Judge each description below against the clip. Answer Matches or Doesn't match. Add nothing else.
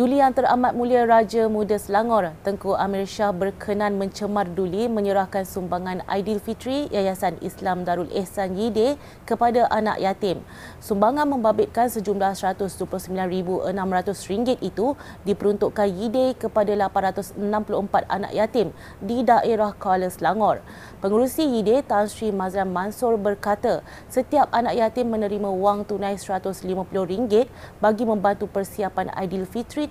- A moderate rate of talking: Matches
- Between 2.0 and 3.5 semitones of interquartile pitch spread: Matches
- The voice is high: Matches